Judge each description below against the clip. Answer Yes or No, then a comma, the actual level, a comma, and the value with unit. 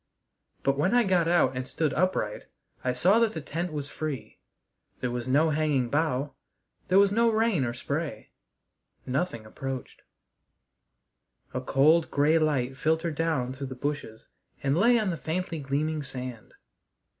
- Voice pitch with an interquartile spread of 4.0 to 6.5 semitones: Yes, average, 4.5 semitones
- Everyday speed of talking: Yes, average, 155 wpm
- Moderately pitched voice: Yes, medium, 150 Hz